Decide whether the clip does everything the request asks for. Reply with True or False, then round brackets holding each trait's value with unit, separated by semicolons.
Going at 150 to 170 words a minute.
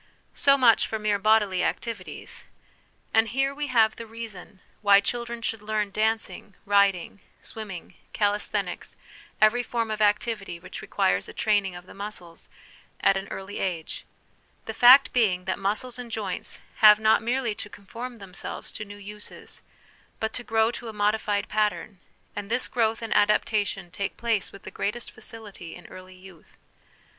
True (160 wpm)